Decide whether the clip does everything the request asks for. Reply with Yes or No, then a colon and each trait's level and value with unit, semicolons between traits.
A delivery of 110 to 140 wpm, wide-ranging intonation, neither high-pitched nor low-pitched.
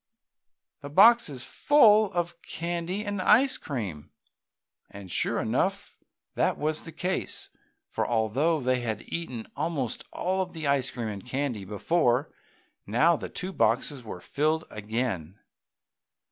Yes: slow, 135 wpm; wide, 6.9 semitones; medium, 145 Hz